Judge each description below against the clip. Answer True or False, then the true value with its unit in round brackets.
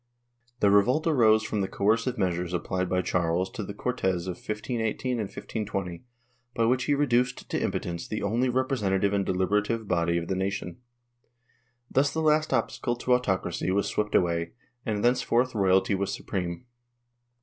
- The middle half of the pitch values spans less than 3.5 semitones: False (4.8 semitones)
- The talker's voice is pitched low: True (105 Hz)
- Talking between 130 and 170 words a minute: True (160 wpm)